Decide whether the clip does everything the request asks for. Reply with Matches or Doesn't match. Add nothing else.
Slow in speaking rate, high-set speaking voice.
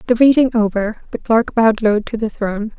Doesn't match